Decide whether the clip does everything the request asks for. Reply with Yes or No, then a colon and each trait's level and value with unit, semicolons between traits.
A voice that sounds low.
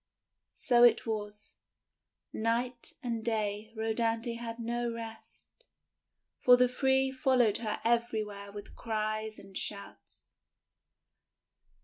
No: high, 230 Hz